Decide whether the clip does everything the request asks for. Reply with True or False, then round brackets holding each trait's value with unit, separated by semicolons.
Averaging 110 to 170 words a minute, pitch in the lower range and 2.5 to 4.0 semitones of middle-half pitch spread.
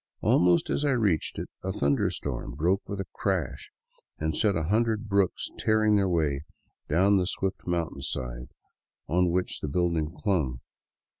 False (155 wpm; 90 Hz; 4.4 semitones)